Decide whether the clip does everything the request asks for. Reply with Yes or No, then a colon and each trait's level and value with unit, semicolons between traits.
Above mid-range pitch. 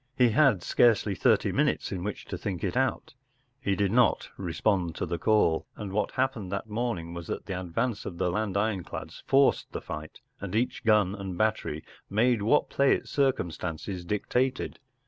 No: low, 105 Hz